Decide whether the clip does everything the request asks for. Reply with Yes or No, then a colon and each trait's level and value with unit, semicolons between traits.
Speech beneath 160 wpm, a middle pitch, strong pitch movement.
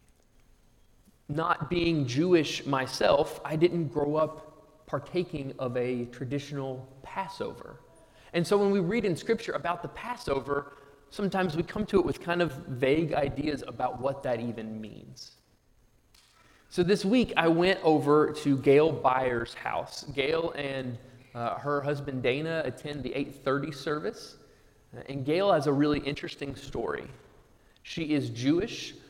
No: average, 140 wpm; medium, 145 Hz; average, 4.0 semitones